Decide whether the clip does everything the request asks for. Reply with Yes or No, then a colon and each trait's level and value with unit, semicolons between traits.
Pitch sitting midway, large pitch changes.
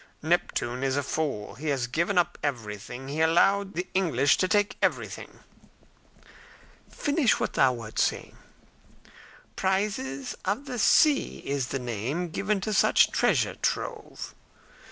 Yes: medium, 160 Hz; wide, 6.9 semitones